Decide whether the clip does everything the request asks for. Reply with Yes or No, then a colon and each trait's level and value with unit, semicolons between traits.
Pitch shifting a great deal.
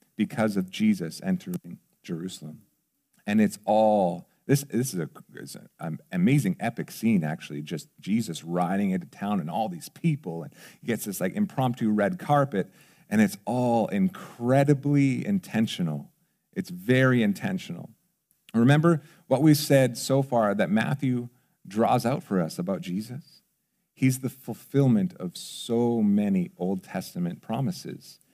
Yes: wide, 7.7 semitones